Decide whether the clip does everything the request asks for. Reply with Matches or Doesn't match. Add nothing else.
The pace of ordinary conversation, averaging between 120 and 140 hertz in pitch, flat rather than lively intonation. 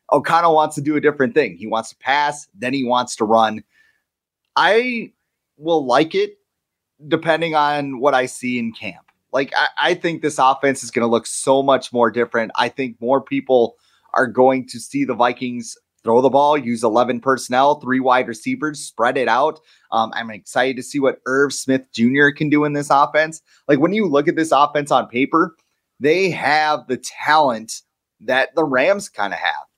Doesn't match